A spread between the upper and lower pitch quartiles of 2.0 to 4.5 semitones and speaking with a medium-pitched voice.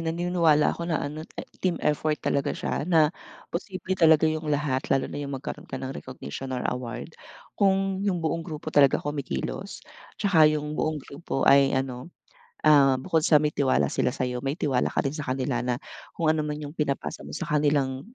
Yes: average, 3.0 semitones; medium, 150 Hz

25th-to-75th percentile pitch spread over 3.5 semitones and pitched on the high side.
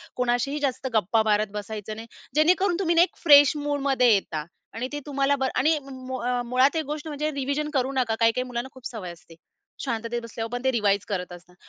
Yes: average, 4.2 semitones; very high, 255 Hz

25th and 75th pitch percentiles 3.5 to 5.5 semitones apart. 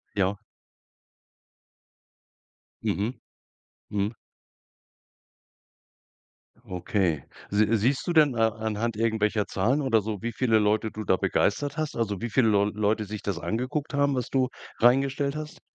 Yes: average, 4.0 semitones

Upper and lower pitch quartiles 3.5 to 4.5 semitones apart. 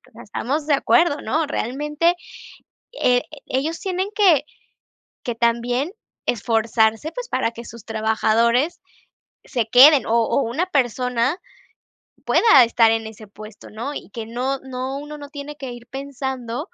Yes: average, 4.2 semitones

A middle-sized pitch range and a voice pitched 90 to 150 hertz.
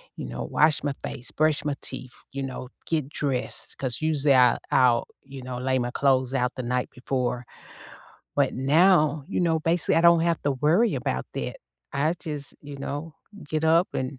Yes: average, 3.5 semitones; medium, 140 Hz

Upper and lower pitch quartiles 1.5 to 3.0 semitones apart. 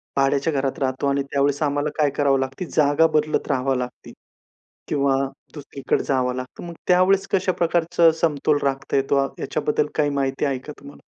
Yes: narrow, 2.6 semitones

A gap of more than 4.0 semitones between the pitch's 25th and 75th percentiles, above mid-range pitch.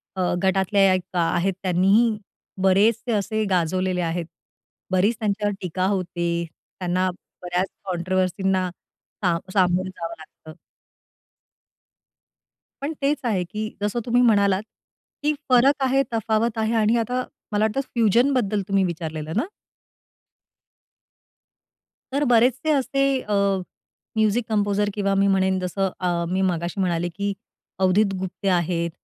No: average, 3.3 semitones; high, 195 Hz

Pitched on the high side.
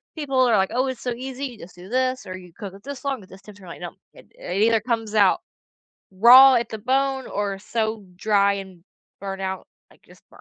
Yes: high, 220 Hz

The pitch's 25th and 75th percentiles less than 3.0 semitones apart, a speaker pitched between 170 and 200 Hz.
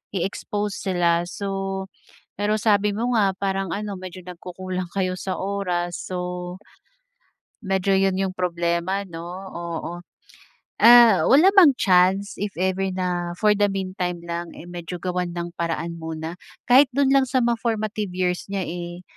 Yes: narrow, 2.6 semitones; medium, 185 Hz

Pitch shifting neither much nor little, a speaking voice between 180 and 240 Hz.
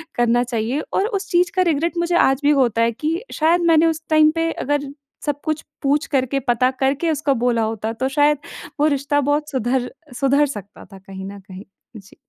No: average, 4.4 semitones; very high, 280 Hz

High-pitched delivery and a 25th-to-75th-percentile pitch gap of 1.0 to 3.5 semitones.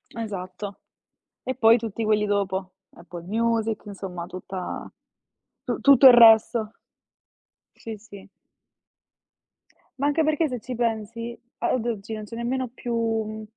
Yes: high, 225 Hz; average, 2.7 semitones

